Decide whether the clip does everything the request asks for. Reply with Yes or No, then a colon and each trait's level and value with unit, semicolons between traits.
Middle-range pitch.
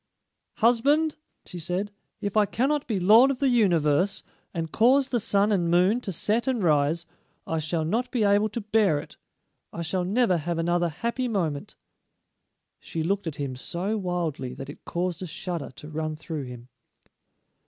Yes: medium, 180 Hz